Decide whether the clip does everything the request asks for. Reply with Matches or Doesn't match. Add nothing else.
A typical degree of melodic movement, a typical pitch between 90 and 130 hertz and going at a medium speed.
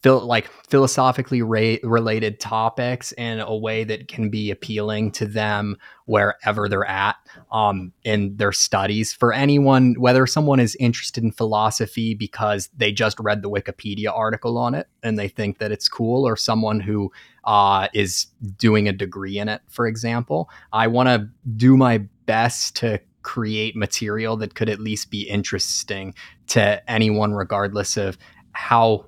Doesn't match